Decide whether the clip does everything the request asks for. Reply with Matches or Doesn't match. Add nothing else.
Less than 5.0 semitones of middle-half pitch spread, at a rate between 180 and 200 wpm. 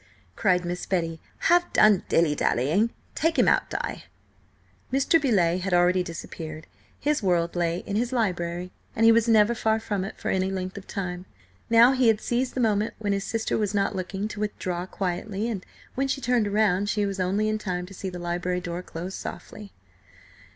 Matches